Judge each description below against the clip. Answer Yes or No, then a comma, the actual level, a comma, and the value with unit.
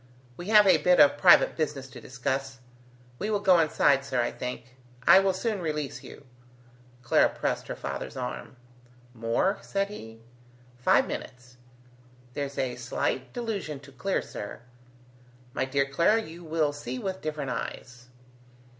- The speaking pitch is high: No, medium, 145 Hz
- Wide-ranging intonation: Yes, wide, 6.2 semitones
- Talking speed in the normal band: Yes, average, 150 wpm